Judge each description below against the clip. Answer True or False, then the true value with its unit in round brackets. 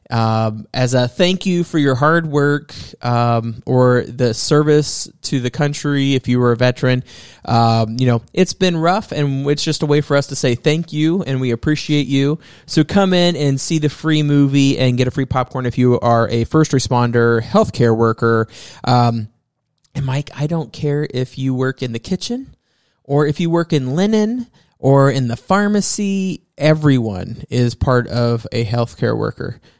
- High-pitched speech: False (135 Hz)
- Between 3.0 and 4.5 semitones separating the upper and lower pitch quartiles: True (4.0 semitones)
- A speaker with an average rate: True (185 wpm)